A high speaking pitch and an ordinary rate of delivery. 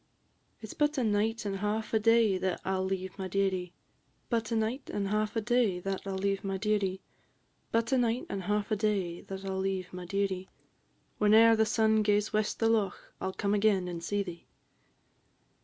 No: high, 205 Hz; fast, 210 wpm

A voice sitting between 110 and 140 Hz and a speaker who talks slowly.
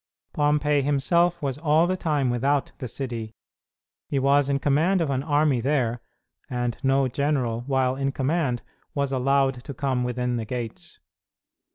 No: low, 135 Hz; average, 155 wpm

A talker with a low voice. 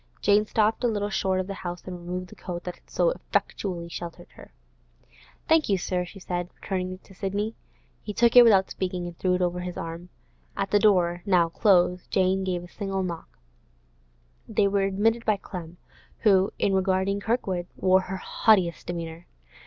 No: medium, 185 Hz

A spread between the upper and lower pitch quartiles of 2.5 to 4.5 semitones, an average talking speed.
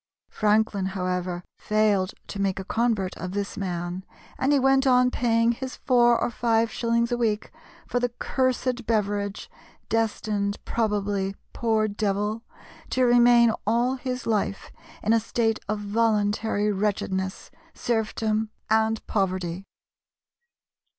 No: average, 2.8 semitones; slow, 125 wpm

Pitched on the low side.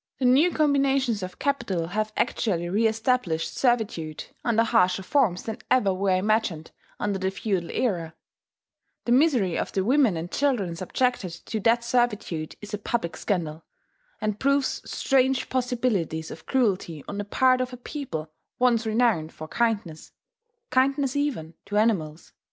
No: high, 215 Hz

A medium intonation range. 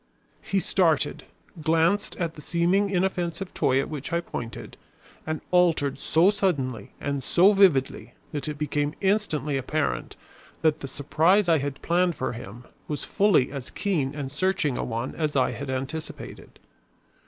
Yes: average, 4.5 semitones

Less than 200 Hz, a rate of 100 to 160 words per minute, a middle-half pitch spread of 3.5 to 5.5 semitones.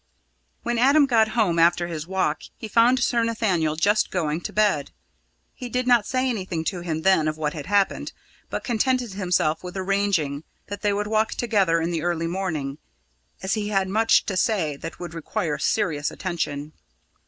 No: high, 190 Hz; average, 180 wpm; average, 5.1 semitones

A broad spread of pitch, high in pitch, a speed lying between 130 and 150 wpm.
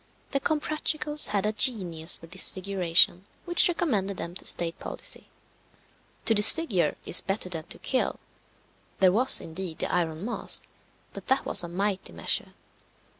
Yes: wide, 6.1 semitones; high, 195 Hz; average, 145 wpm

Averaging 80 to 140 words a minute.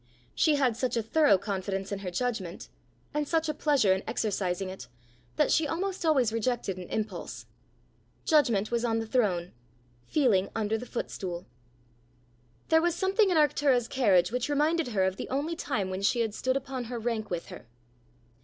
No: average, 175 wpm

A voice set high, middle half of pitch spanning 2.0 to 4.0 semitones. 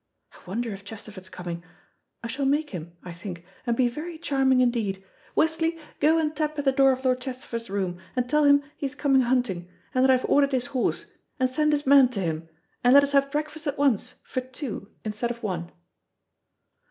No: very high, 255 Hz; average, 5.3 semitones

